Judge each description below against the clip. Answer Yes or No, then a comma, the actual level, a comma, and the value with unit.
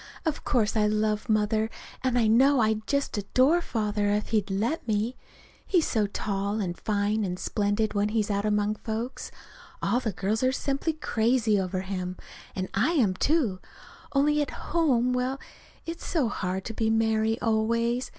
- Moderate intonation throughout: Yes, average, 3.5 semitones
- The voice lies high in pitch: Yes, high, 220 Hz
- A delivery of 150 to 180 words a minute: Yes, average, 170 wpm